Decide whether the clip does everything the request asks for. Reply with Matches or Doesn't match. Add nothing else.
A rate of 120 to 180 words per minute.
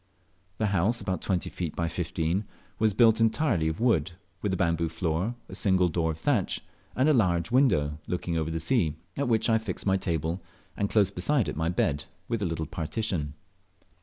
Doesn't match